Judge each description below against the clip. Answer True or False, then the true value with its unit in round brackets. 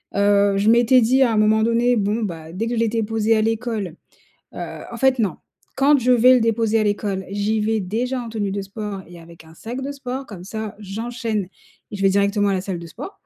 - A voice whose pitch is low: False (220 Hz)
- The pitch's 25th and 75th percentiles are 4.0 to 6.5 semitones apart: False (2.7 semitones)